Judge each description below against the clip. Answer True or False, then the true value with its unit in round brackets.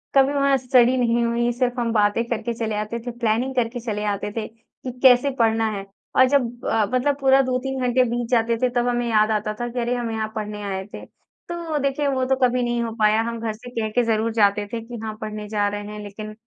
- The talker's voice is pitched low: False (235 Hz)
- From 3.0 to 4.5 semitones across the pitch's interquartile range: False (2.6 semitones)